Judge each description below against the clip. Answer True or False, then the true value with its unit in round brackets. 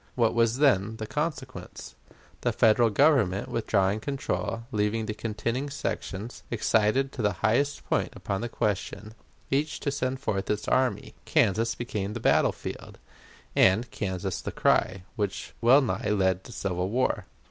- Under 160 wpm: True (145 wpm)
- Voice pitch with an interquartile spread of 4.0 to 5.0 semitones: True (4.3 semitones)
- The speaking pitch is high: False (110 Hz)